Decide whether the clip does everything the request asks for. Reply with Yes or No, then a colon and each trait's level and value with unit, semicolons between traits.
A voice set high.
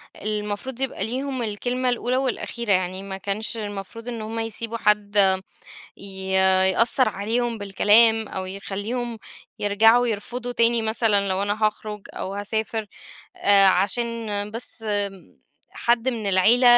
Yes: high, 220 Hz